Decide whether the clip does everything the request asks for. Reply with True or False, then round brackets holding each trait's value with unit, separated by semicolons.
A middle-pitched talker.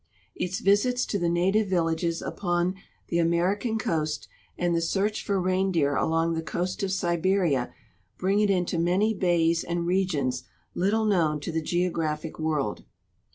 True (175 Hz)